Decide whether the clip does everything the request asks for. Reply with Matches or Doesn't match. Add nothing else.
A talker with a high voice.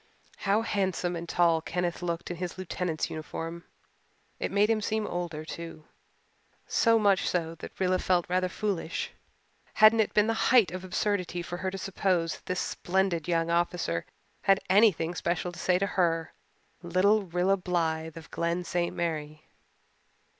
Doesn't match